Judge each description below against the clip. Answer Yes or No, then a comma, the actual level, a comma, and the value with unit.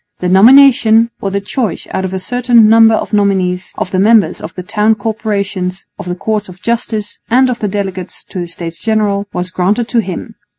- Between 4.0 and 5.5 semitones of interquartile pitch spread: No, average, 3.2 semitones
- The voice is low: No, high, 205 Hz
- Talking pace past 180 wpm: Yes, fast, 205 wpm